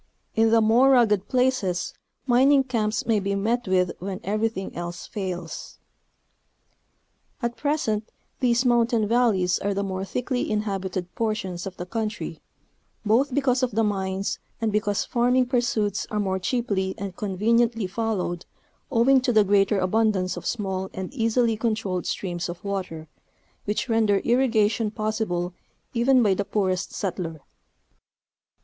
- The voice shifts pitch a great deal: No, average, 3.8 semitones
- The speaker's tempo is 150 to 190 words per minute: No, average, 140 wpm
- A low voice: No, high, 215 Hz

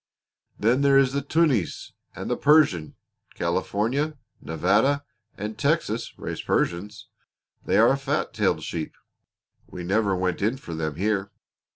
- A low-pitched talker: Yes, low, 110 Hz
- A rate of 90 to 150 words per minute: Yes, average, 140 wpm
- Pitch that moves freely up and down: Yes, wide, 7.2 semitones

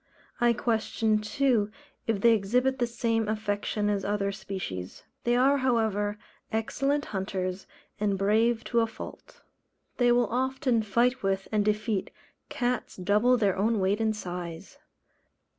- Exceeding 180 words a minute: No, average, 140 wpm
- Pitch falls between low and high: No, high, 215 Hz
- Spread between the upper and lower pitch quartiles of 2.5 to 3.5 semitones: Yes, average, 3.2 semitones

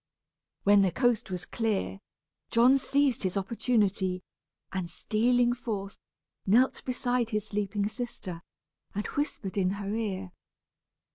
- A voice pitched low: No, high, 210 Hz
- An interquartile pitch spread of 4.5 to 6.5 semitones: No, average, 3.9 semitones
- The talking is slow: Yes, slow, 120 wpm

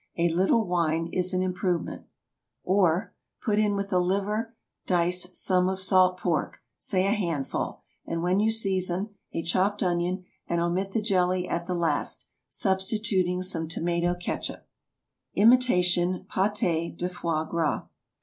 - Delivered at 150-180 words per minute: No, slow, 135 wpm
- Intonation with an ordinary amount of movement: No, narrow, 2.2 semitones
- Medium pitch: Yes, medium, 180 Hz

